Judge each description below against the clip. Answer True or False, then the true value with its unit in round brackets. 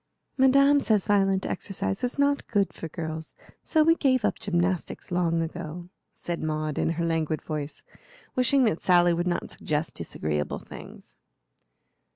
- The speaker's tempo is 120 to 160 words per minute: True (150 wpm)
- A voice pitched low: False (175 Hz)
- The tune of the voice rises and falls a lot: True (6.5 semitones)